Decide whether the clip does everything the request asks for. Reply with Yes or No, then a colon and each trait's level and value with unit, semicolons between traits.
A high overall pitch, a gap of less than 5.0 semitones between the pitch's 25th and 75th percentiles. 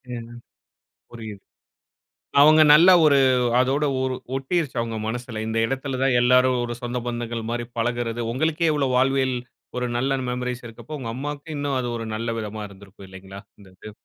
No: low, 125 Hz; average, 2.9 semitones